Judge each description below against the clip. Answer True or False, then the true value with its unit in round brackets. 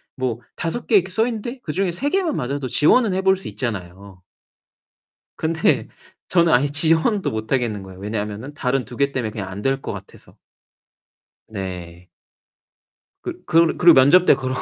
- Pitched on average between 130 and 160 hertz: True (135 Hz)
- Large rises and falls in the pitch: True (8.5 semitones)